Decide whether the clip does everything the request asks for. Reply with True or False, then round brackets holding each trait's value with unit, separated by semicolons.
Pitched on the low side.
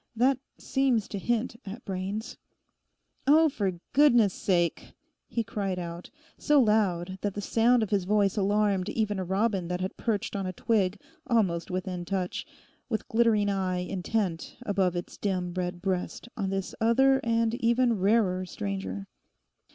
False (200 Hz)